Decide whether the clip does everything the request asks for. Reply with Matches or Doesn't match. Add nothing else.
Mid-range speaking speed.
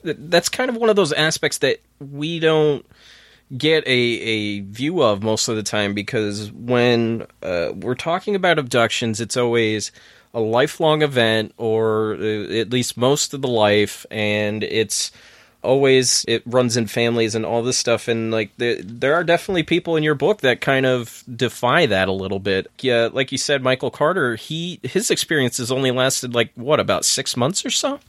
Matches